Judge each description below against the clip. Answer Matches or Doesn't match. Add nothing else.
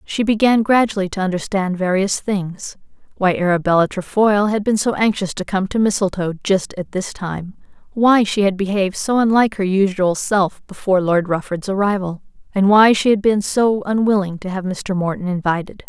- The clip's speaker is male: Doesn't match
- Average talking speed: Matches